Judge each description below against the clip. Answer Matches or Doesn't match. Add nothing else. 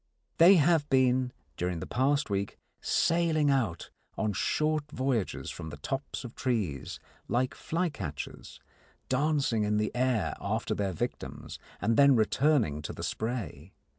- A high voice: Doesn't match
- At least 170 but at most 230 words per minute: Doesn't match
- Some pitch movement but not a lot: Doesn't match